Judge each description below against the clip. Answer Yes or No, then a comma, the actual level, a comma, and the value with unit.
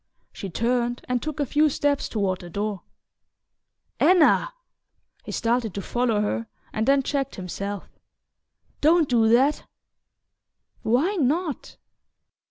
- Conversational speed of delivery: No, slow, 120 wpm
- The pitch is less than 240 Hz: No, high, 245 Hz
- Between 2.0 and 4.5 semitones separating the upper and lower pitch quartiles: No, wide, 5.6 semitones